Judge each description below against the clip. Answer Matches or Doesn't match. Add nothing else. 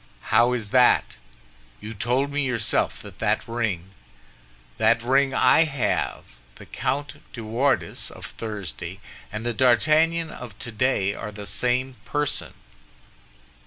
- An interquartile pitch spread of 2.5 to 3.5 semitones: Doesn't match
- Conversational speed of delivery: Doesn't match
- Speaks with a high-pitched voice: Doesn't match